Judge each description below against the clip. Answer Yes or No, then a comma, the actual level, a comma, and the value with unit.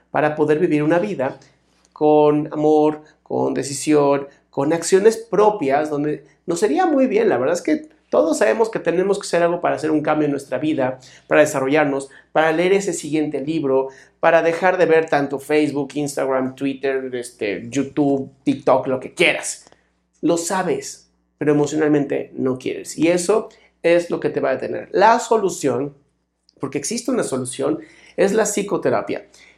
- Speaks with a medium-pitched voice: Yes, medium, 150 Hz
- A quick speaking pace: No, average, 160 wpm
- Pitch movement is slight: No, average, 3.7 semitones